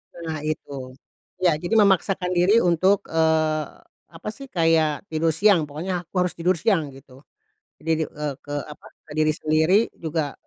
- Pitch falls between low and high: Yes, medium, 160 Hz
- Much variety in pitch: No, average, 2.8 semitones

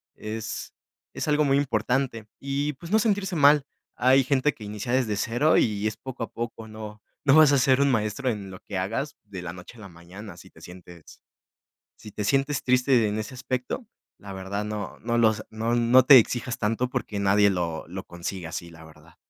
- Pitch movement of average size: Yes, average, 4.7 semitones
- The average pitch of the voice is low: Yes, low, 115 Hz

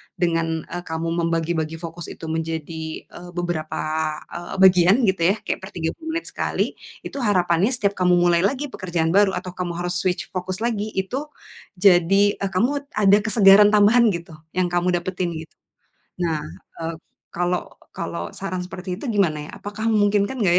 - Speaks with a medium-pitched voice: Yes, medium, 180 Hz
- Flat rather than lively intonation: No, average, 3.2 semitones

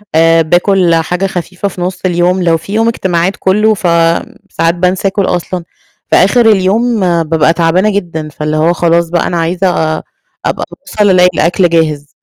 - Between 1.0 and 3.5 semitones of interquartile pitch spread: Yes, narrow, 2.6 semitones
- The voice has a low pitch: No, medium, 175 Hz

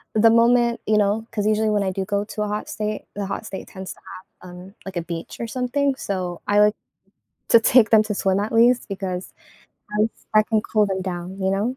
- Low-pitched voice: No, high, 210 Hz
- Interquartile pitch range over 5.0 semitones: No, narrow, 2.6 semitones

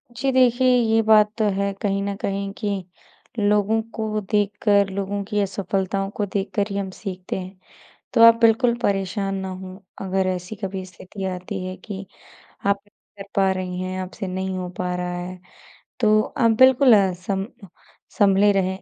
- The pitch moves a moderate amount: No, narrow, 2.1 semitones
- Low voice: No, high, 195 Hz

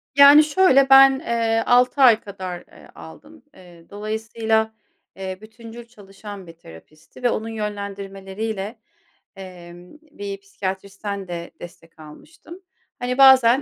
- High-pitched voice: Yes, high, 215 Hz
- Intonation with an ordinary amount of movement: Yes, average, 4.4 semitones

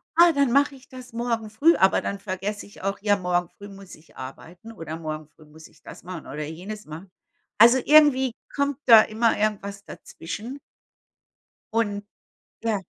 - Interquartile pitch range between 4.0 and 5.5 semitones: Yes, average, 5.0 semitones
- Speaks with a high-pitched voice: Yes, high, 205 Hz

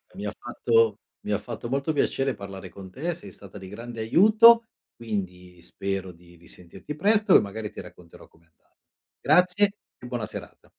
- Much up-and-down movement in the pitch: Yes, wide, 7.8 semitones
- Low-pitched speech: Yes, low, 110 Hz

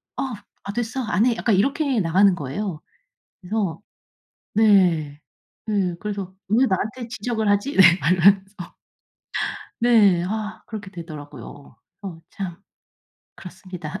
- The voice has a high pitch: Yes, high, 200 Hz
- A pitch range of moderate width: Yes, average, 3.7 semitones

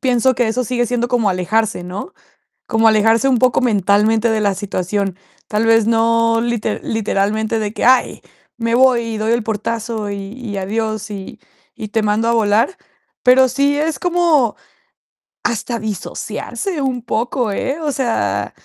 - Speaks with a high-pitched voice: Yes, high, 225 Hz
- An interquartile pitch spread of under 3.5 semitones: Yes, average, 2.7 semitones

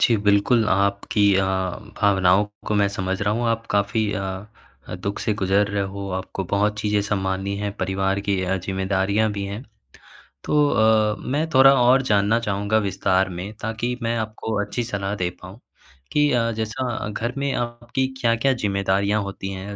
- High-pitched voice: No, low, 105 Hz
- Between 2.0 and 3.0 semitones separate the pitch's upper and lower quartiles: Yes, average, 2.7 semitones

